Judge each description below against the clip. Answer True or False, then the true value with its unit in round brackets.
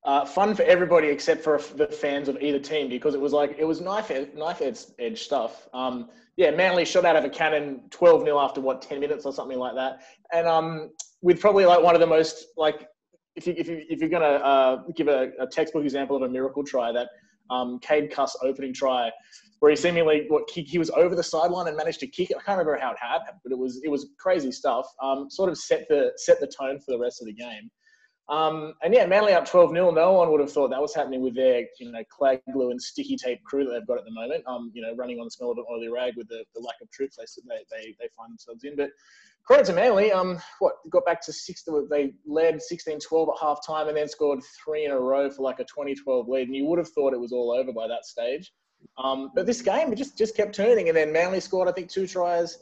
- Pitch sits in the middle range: True (155 Hz)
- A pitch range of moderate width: True (4.8 semitones)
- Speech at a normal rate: False (260 wpm)